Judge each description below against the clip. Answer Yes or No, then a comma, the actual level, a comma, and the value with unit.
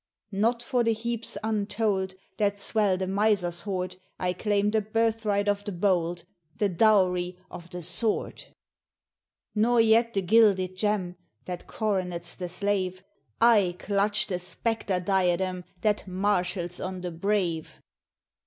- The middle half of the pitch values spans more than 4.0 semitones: No, average, 2.9 semitones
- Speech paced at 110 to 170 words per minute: Yes, slow, 135 wpm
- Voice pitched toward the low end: No, high, 200 Hz